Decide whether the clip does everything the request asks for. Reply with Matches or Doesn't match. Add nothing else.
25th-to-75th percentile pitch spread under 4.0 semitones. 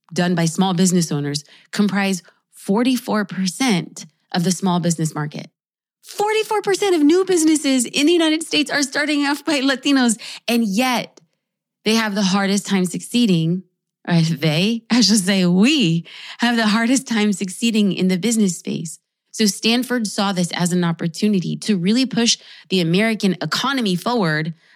Doesn't match